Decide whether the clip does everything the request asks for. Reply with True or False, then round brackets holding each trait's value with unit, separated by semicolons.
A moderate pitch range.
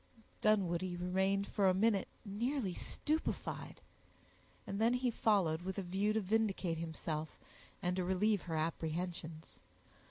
True (3.5 semitones)